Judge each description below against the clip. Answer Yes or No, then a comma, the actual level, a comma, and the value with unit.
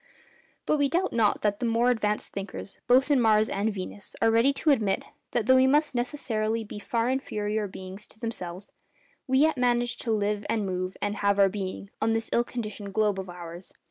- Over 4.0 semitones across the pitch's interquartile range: No, average, 3.2 semitones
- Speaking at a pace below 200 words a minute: No, fast, 205 wpm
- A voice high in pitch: Yes, high, 220 Hz